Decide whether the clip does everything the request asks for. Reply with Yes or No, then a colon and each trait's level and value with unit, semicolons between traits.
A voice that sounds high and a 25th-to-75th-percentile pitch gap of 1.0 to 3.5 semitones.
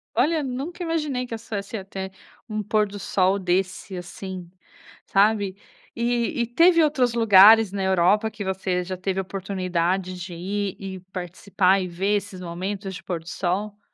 Yes: high, 195 Hz; average, 3.1 semitones